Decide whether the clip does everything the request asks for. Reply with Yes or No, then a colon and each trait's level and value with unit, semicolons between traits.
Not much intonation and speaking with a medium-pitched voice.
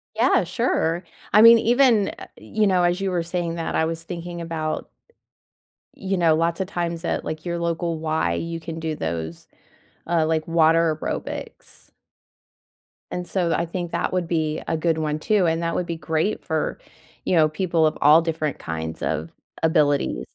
Yes: narrow, 1.9 semitones; medium, 165 Hz